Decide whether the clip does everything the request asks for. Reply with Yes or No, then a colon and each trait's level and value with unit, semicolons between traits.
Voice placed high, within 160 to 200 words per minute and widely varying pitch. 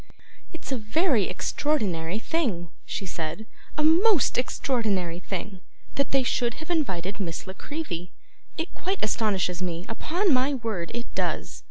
No: high, 225 Hz; average, 145 wpm; wide, 8.5 semitones